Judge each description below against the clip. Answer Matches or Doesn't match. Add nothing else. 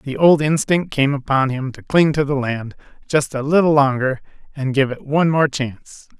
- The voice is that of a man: Matches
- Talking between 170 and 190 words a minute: Doesn't match